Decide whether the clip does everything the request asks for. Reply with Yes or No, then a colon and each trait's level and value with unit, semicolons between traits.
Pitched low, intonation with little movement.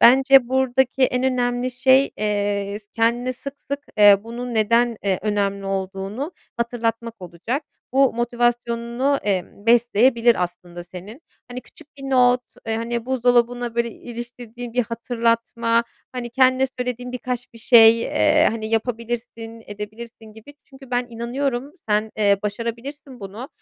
No: high, 235 Hz; narrow, 2.1 semitones